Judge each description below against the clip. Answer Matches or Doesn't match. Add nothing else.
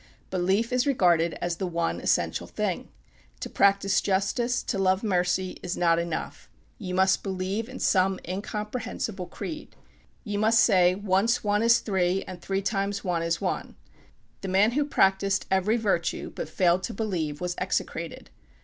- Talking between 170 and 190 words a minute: Doesn't match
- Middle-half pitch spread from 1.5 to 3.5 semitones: Matches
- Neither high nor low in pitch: Doesn't match